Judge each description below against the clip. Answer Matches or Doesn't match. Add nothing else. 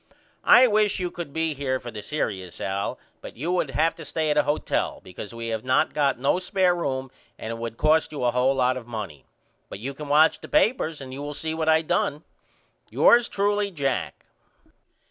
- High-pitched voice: Doesn't match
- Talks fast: Matches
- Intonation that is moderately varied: Matches